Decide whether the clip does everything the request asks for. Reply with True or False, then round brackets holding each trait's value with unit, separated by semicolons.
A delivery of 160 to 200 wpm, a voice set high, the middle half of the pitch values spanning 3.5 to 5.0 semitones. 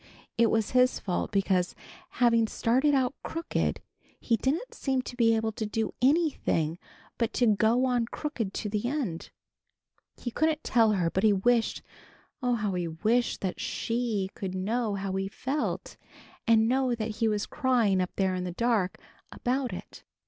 True (170 wpm; 225 Hz; 4.0 semitones)